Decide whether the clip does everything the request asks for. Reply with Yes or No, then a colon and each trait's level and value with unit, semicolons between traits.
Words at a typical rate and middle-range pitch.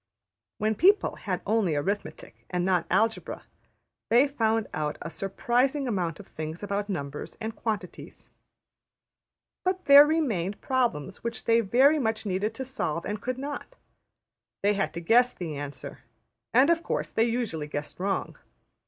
No: average, 150 wpm; high, 220 Hz